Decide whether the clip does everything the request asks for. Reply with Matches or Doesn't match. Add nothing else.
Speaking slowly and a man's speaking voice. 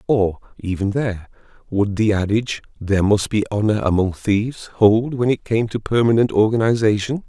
Doesn't match